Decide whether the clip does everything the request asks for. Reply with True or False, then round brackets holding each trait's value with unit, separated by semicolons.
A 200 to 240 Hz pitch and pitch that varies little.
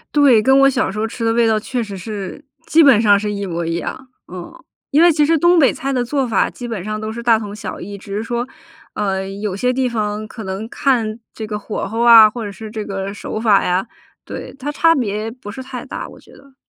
False (220 Hz; 3.7 semitones)